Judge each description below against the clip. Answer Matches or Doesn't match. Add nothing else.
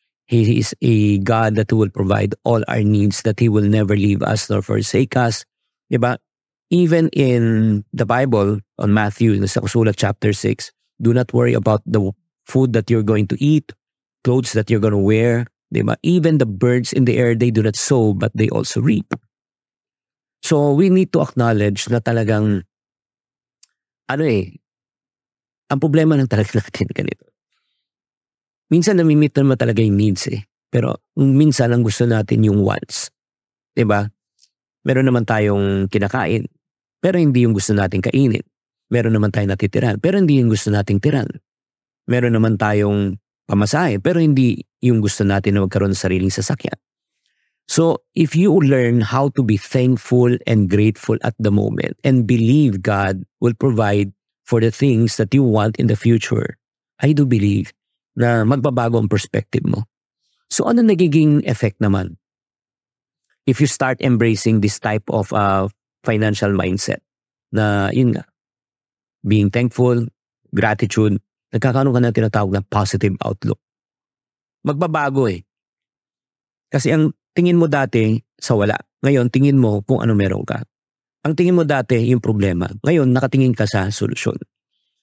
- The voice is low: Matches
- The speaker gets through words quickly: Doesn't match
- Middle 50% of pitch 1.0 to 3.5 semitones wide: Doesn't match